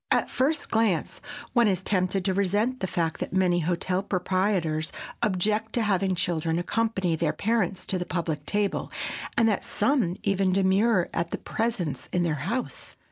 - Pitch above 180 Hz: Yes, high, 190 Hz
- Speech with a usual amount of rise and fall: Yes, average, 3.6 semitones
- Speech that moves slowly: No, average, 170 wpm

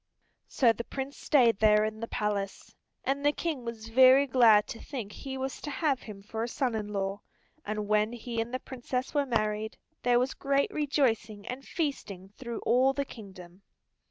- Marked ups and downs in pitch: No, average, 4.0 semitones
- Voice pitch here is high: Yes, high, 235 Hz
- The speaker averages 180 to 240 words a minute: Yes, average, 185 wpm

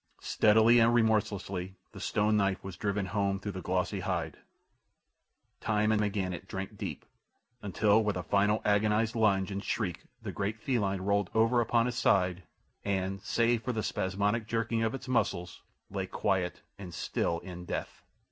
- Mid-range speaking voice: No, low, 100 Hz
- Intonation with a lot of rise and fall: No, average, 2.7 semitones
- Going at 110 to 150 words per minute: No, average, 160 wpm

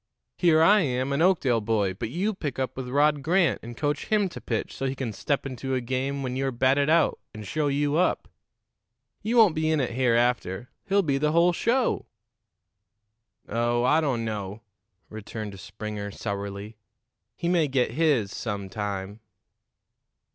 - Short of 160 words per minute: No, average, 170 wpm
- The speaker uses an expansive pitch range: Yes, wide, 5.8 semitones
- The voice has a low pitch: Yes, low, 130 Hz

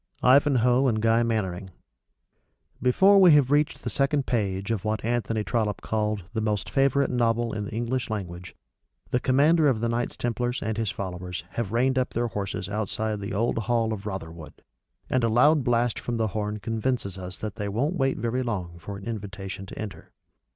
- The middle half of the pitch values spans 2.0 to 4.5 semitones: Yes, average, 3.5 semitones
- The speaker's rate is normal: Yes, average, 185 wpm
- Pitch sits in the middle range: No, low, 115 Hz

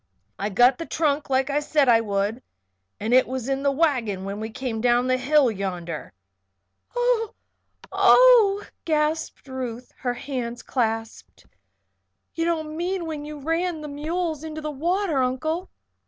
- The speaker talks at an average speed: Yes, average, 155 wpm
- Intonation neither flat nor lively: Yes, average, 4.9 semitones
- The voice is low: No, very high, 275 Hz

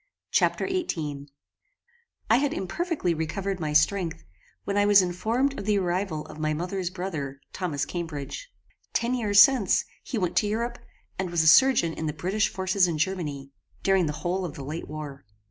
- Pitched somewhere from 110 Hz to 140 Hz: No, medium, 180 Hz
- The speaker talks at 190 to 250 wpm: No, average, 175 wpm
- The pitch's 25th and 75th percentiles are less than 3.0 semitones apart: No, average, 4.7 semitones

